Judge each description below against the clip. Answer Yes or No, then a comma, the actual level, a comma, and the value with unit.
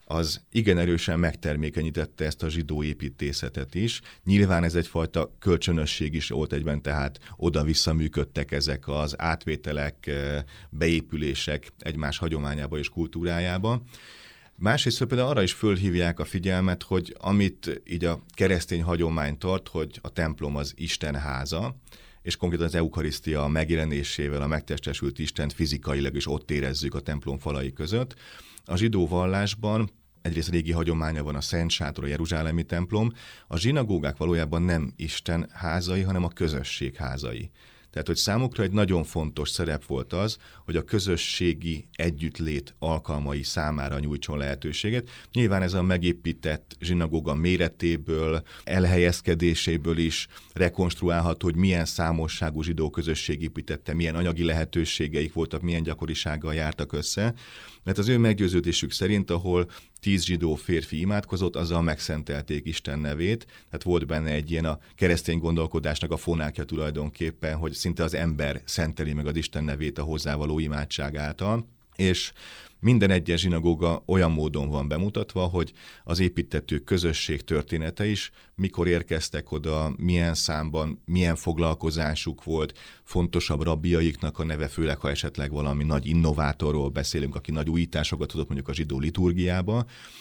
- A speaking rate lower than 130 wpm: No, average, 135 wpm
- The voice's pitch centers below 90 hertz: Yes, very low, 80 Hz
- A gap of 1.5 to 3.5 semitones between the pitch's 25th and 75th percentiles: Yes, average, 2.9 semitones